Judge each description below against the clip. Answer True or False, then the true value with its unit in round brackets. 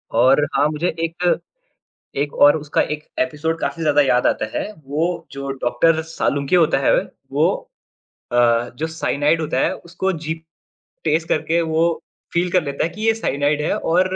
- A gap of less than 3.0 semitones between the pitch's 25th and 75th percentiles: True (2.6 semitones)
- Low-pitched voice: False (160 Hz)